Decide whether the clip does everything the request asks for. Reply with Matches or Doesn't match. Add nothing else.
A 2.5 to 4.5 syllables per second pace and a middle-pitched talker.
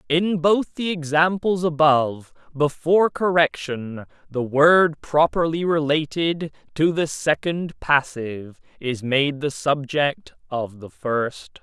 Matches